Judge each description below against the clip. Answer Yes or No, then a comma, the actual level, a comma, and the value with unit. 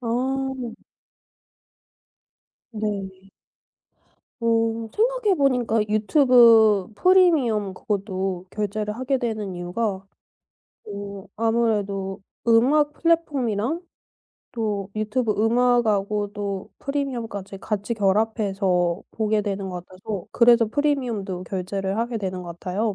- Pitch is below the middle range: No, high, 215 Hz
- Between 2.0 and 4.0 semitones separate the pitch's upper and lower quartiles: Yes, average, 3.7 semitones